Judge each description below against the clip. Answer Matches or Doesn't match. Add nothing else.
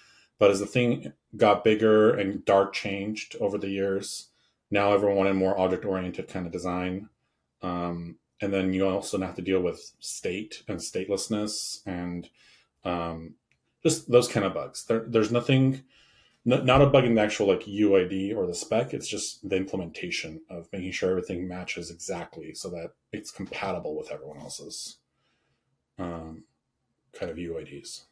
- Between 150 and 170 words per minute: Matches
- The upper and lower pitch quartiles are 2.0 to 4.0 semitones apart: Matches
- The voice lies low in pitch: Matches